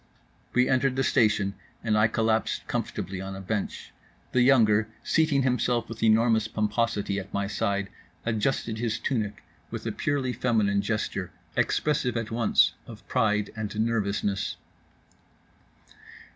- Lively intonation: No, average, 2.7 semitones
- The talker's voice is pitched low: Yes, low, 110 Hz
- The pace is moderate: No, slow, 130 wpm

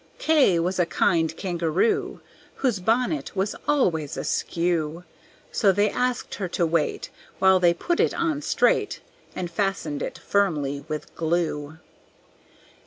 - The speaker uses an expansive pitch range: No, average, 4.2 semitones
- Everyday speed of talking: No, slow, 130 wpm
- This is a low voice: No, medium, 180 Hz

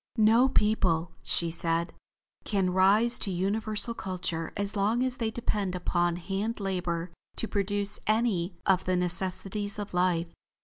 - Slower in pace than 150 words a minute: Yes, average, 140 wpm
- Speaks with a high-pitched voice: Yes, high, 195 Hz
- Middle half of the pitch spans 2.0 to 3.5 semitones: Yes, average, 3.1 semitones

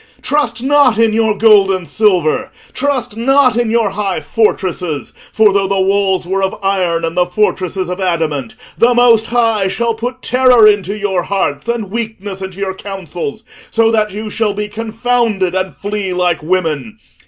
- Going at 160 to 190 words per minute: Yes, average, 170 wpm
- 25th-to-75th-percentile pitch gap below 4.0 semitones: Yes, average, 3.4 semitones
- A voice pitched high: Yes, high, 205 Hz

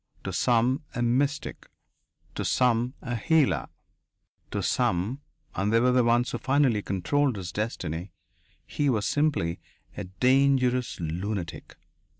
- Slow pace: Yes, slow, 130 wpm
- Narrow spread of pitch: No, average, 5.1 semitones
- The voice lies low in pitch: Yes, low, 120 Hz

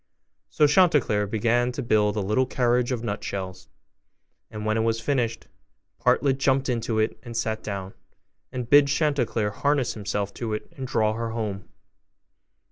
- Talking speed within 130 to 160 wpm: Yes, average, 155 wpm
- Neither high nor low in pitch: No, low, 115 Hz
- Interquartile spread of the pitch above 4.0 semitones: No, average, 3.4 semitones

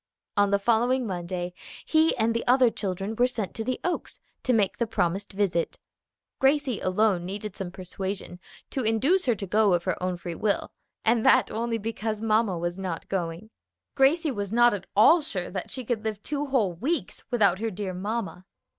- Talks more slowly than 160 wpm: No, average, 190 wpm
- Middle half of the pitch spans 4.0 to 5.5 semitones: Yes, average, 4.3 semitones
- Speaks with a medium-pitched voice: No, high, 215 Hz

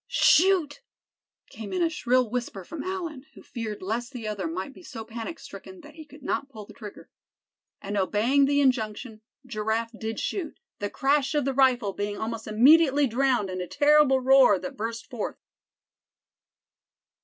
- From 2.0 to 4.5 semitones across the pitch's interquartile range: No, average, 4.9 semitones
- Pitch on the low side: No, very high, 250 Hz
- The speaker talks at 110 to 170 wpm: Yes, average, 165 wpm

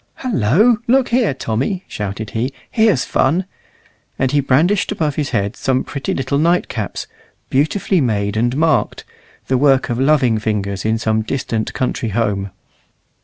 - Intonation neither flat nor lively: No, wide, 6.5 semitones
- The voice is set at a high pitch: No, low, 130 Hz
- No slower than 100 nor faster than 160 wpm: Yes, average, 150 wpm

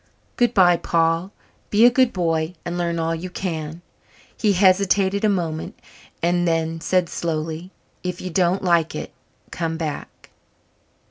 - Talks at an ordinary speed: Yes, average, 145 wpm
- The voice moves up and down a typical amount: No, narrow, 2.3 semitones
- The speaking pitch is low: No, medium, 175 Hz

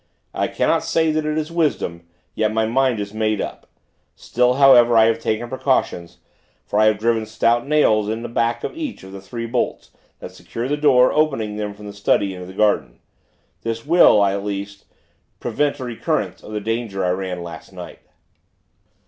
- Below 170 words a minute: No, average, 190 wpm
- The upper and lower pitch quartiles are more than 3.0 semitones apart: Yes, average, 3.8 semitones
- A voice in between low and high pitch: No, low, 110 Hz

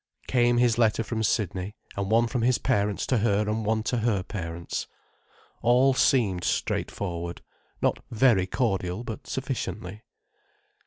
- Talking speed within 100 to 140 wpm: Yes, slow, 135 wpm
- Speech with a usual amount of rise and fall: Yes, average, 3.6 semitones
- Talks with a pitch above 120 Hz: No, low, 110 Hz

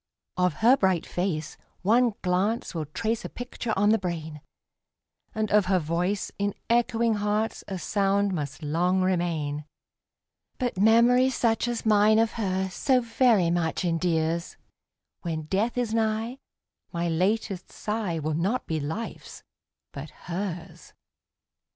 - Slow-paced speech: Yes, slow, 125 wpm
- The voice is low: No, high, 195 Hz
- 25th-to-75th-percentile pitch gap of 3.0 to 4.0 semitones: No, average, 4.8 semitones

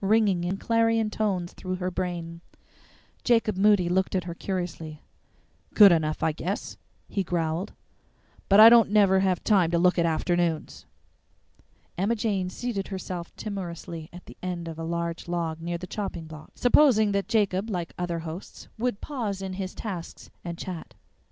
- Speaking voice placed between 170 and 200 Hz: Yes, medium, 185 Hz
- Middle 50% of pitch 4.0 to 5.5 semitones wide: No, average, 3.3 semitones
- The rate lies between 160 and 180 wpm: Yes, average, 165 wpm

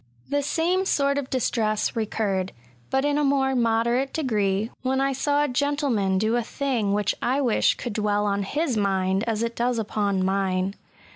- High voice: Yes, high, 230 Hz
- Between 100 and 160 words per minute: No, average, 180 wpm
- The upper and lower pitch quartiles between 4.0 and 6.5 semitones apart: Yes, average, 5.1 semitones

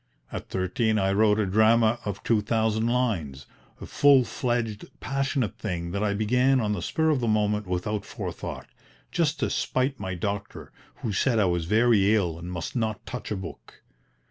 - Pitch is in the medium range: No, low, 110 Hz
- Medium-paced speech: Yes, average, 175 wpm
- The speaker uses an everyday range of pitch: Yes, average, 3.5 semitones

